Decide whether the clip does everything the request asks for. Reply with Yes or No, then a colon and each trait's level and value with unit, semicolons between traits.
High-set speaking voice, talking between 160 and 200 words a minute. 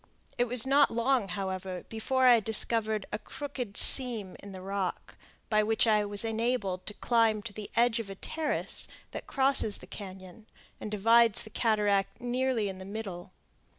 Yes: high, 220 Hz; average, 170 wpm